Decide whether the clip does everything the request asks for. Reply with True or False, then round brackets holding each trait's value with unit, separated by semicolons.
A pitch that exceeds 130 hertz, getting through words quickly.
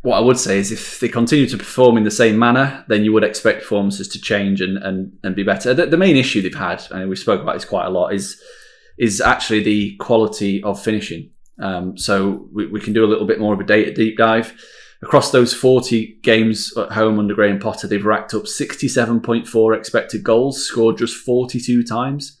False (110 Hz; 215 wpm)